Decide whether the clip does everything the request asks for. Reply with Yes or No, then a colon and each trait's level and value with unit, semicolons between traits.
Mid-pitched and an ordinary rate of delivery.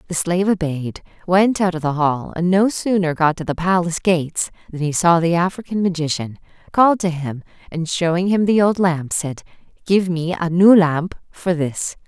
Yes: medium, 175 Hz; average, 195 wpm